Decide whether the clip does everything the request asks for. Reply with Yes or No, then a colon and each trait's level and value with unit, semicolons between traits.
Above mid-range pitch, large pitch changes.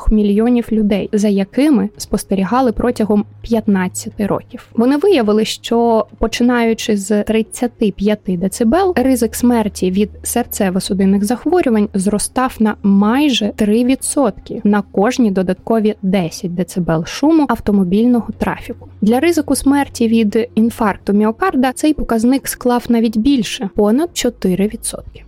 No: high, 220 Hz; average, 2.9 semitones